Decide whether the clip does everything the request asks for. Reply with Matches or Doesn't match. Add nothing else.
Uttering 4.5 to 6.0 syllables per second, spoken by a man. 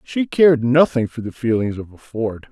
Matches